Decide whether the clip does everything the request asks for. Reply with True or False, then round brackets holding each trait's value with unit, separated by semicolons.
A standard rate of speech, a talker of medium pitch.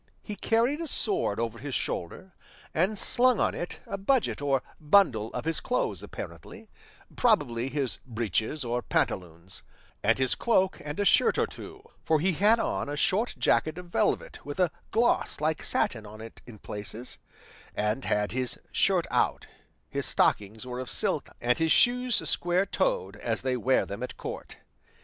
True (170 wpm; 145 Hz)